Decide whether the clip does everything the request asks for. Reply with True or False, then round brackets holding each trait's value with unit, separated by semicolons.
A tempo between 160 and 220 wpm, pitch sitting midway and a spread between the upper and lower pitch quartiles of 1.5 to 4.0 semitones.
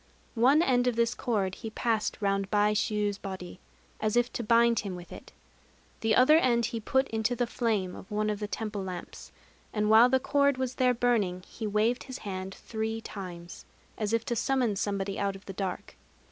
False (195 wpm; 220 Hz; 3.3 semitones)